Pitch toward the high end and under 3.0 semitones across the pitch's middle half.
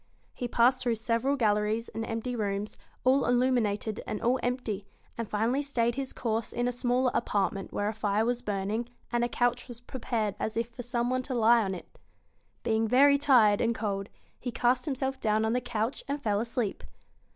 Yes: high, 235 Hz; narrow, 2.5 semitones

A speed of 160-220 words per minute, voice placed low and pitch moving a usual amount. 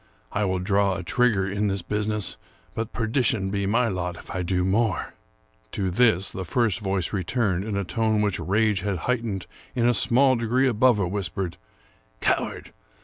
Yes: average, 190 wpm; low, 100 Hz; average, 3.3 semitones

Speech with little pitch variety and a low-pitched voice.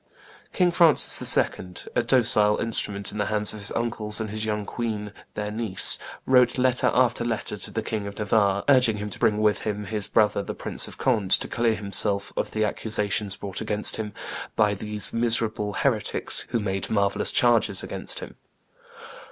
Yes: narrow, 2.1 semitones; low, 105 Hz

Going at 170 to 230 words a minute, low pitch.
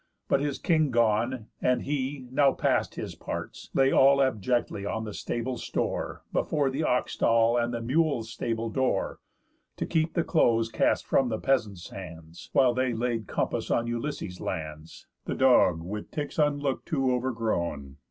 No: average, 155 wpm; low, 120 Hz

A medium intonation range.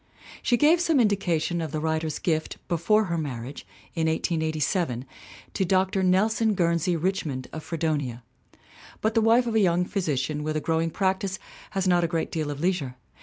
Yes: average, 3.7 semitones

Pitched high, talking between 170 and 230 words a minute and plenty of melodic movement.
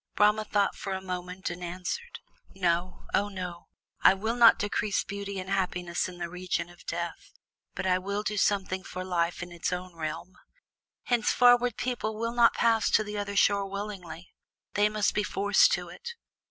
No: high, 195 Hz; average, 180 wpm; average, 2.7 semitones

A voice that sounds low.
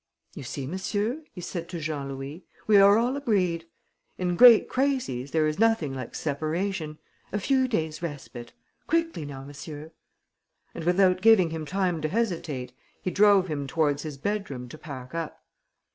No: medium, 165 Hz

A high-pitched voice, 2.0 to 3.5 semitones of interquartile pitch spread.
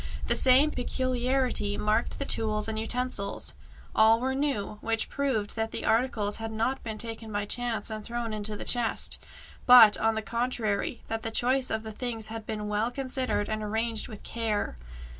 Yes: high, 225 Hz; narrow, 2.5 semitones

